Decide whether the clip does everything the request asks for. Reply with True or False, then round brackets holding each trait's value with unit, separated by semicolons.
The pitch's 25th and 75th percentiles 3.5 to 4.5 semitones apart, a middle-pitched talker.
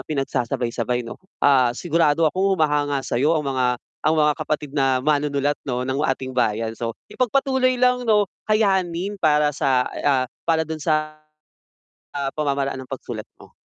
True (3.9 semitones; 145 Hz)